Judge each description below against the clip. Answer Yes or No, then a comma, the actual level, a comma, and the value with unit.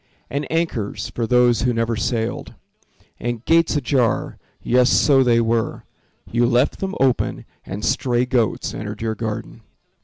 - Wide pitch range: No, narrow, 2.4 semitones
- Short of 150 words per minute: Yes, average, 140 wpm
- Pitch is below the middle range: Yes, low, 120 Hz